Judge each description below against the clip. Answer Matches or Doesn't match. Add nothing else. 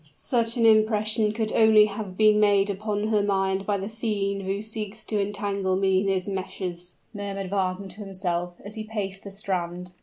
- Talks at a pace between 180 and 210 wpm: Matches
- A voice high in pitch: Matches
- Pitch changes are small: Matches